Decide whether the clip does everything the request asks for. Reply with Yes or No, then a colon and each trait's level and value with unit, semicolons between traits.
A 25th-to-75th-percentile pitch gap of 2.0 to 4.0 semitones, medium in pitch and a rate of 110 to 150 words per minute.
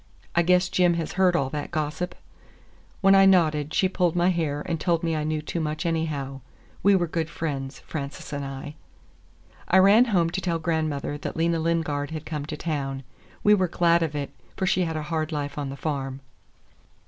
No: average, 2.9 semitones; medium, 160 Hz; average, 200 wpm